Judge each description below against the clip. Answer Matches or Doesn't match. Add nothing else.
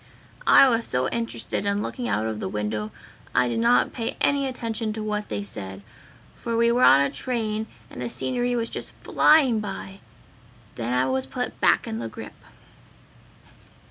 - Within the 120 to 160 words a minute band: Doesn't match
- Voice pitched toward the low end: Doesn't match